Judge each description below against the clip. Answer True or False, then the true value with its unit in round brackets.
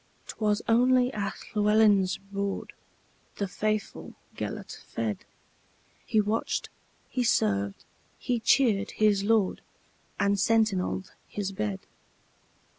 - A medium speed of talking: False (90 wpm)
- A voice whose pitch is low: False (210 Hz)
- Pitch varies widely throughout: False (2.4 semitones)